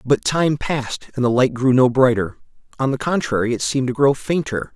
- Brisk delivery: Yes, fast, 215 wpm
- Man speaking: Yes, male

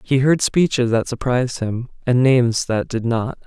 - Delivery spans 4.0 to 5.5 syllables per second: Yes, 4.8 syllables/s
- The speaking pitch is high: No, low, 125 Hz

